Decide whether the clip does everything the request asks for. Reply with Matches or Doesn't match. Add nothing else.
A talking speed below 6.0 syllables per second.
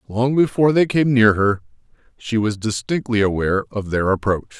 Matches